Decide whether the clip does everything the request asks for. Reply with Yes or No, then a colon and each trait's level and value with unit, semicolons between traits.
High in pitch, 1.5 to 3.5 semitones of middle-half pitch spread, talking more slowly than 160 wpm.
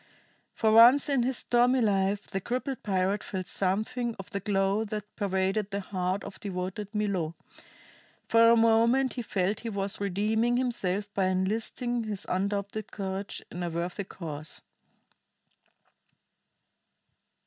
Yes: high, 205 Hz; average, 3.1 semitones; slow, 135 wpm